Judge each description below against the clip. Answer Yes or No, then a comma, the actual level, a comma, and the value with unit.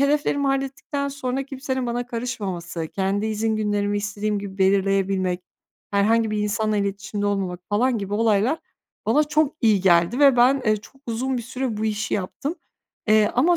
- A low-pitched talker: No, high, 215 Hz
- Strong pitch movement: No, average, 4.4 semitones